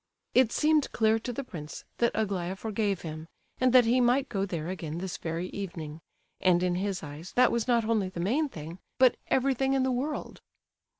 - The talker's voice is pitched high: Yes, high, 205 Hz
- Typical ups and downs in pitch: No, wide, 6.2 semitones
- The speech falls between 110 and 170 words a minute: No, average, 195 wpm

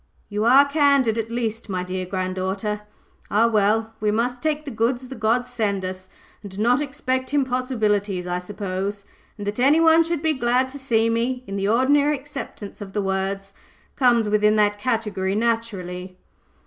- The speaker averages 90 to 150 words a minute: No, average, 170 wpm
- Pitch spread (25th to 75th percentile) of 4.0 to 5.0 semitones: Yes, average, 4.3 semitones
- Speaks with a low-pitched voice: No, high, 225 Hz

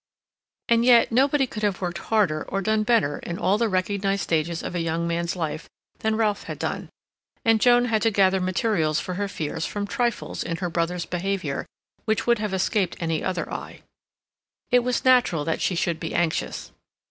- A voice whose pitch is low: No, high, 190 Hz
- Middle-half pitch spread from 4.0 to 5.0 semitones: Yes, average, 4.5 semitones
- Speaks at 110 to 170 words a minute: No, average, 190 wpm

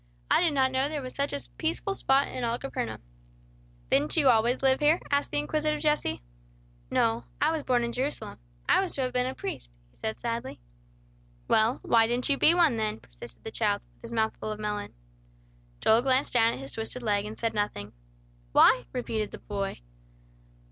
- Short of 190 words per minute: No, average, 195 wpm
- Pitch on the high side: Yes, high, 240 Hz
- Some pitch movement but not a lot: Yes, average, 4.5 semitones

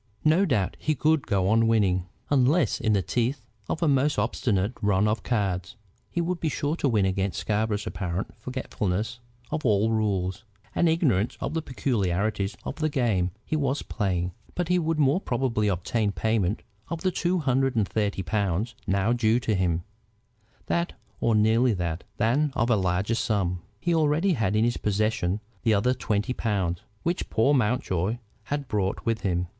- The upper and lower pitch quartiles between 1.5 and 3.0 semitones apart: No, wide, 5.6 semitones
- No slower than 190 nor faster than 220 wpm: No, average, 175 wpm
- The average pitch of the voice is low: Yes, low, 110 Hz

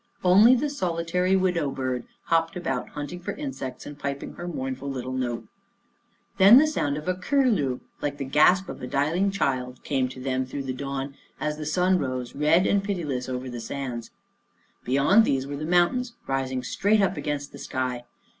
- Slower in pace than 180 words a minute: No, average, 195 wpm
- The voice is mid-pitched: Yes, medium, 145 Hz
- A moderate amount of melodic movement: No, wide, 5.7 semitones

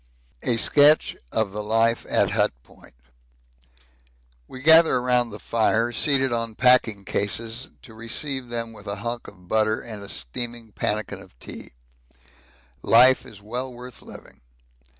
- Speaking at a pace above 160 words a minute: No, average, 150 wpm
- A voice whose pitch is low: Yes, low, 115 Hz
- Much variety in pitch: No, average, 2.7 semitones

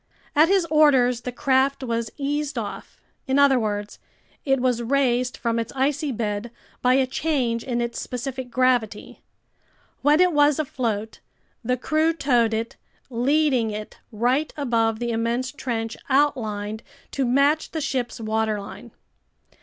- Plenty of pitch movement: No, average, 3.4 semitones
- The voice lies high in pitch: Yes, very high, 250 Hz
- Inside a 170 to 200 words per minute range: No, average, 140 wpm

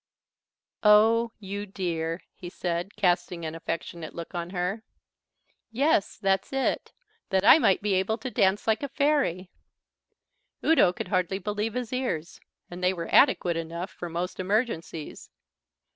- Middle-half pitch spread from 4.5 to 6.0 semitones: No, average, 4.0 semitones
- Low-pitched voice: No, high, 190 Hz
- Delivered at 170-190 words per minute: No, average, 145 wpm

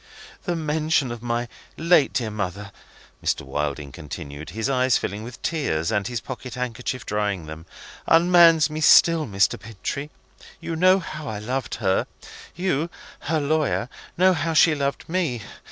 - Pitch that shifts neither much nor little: No, wide, 7.3 semitones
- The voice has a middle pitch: No, low, 125 Hz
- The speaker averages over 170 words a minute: No, average, 155 wpm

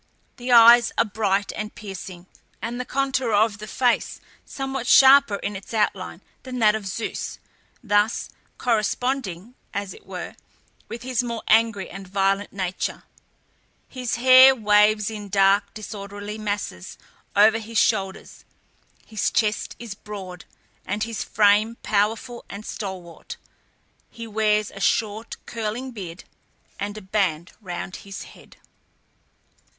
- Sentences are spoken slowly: Yes, slow, 130 wpm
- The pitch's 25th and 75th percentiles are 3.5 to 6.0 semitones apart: No, narrow, 2.6 semitones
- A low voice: No, high, 210 Hz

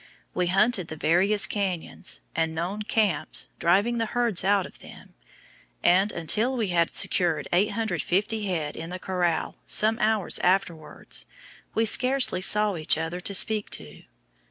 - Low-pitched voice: No, high, 190 Hz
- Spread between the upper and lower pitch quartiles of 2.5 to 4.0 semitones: Yes, average, 3.7 semitones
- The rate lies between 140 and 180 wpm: Yes, average, 145 wpm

